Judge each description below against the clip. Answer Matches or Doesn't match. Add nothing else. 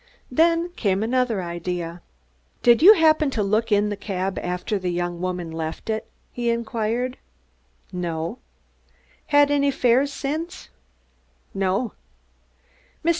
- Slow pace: Matches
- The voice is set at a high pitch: Matches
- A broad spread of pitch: Matches